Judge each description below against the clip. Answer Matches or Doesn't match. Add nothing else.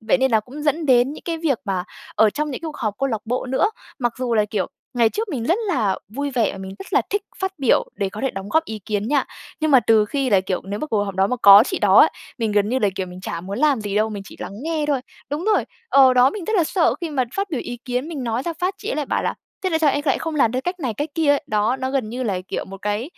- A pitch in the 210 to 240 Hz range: Doesn't match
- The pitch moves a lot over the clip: Matches